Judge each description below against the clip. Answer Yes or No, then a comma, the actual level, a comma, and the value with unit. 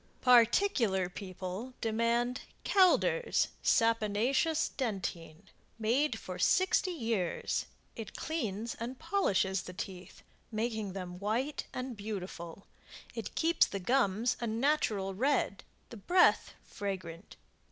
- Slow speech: Yes, slow, 105 wpm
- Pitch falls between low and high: No, high, 225 Hz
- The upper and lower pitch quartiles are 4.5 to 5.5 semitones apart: Yes, average, 5.2 semitones